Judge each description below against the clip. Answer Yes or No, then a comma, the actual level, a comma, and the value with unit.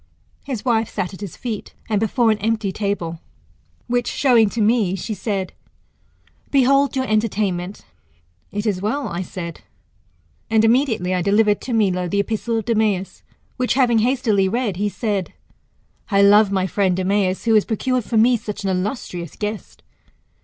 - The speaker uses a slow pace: No, average, 160 wpm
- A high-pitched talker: Yes, high, 210 Hz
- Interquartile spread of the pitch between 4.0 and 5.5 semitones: No, average, 3.2 semitones